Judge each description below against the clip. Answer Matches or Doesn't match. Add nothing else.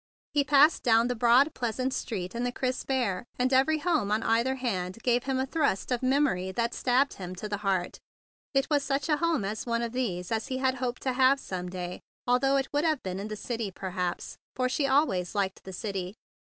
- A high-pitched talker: Matches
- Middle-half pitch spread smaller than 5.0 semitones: Doesn't match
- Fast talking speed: Matches